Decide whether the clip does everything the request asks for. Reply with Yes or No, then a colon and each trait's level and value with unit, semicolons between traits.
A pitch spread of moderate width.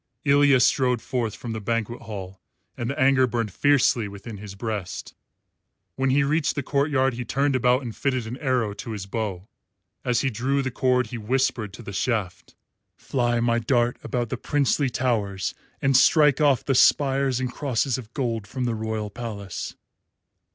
Yes: average, 3.3 semitones